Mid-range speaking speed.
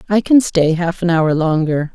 No: fast, 215 wpm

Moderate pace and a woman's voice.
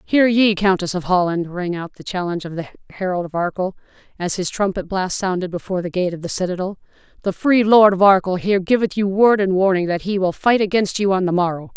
No: fast, 230 wpm; female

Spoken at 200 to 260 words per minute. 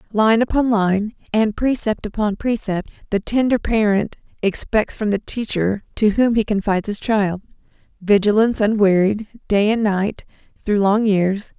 No: average, 145 wpm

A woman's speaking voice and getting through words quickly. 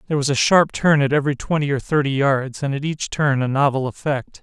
No: male; fast, 245 wpm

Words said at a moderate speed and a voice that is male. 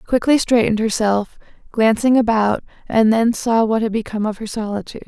No: average, 175 wpm; female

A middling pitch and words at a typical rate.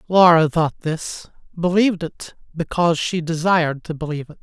Yes: medium, 165 Hz; average, 150 wpm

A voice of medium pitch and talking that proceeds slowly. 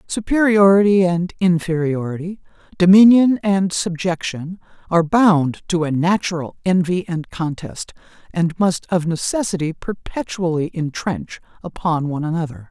Yes: medium, 175 Hz; slow, 110 wpm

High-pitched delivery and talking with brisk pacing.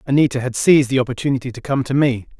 No: low, 130 Hz; fast, 225 wpm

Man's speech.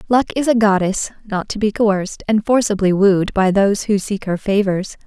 No: female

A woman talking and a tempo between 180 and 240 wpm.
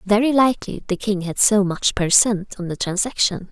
Yes: female; fast, 205 wpm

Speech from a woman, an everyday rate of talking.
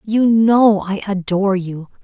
Yes: female; average, 150 wpm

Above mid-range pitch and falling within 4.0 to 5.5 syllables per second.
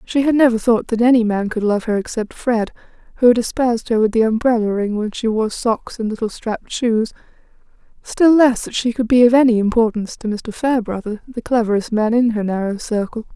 No: high, 225 Hz; 5.7 syllables/s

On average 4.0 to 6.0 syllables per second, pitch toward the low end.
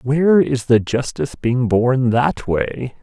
No: 3.8 syllables/s; low, 130 Hz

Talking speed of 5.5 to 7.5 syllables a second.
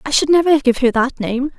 Yes: 5.6 syllables/s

